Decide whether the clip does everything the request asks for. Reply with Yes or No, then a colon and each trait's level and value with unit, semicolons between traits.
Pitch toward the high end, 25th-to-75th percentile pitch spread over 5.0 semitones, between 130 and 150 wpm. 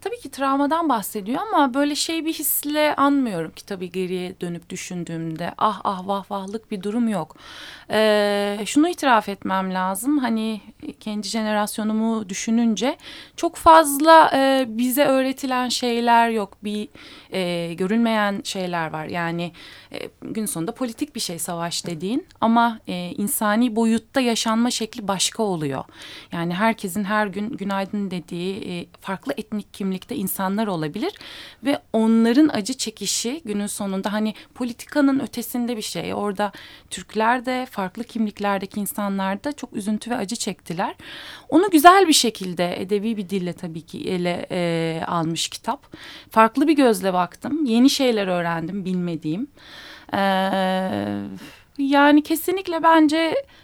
Yes: high, 215 Hz; wide, 5.6 semitones; average, 135 wpm